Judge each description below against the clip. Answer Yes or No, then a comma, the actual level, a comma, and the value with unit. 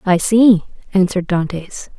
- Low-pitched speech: No, high, 190 Hz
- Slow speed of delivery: Yes, slow, 120 wpm